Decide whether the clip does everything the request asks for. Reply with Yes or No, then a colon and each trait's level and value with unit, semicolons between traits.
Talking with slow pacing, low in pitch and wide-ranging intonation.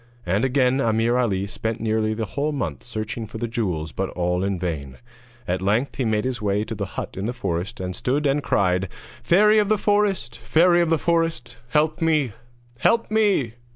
No: average, 195 wpm; low, 115 Hz; wide, 7.3 semitones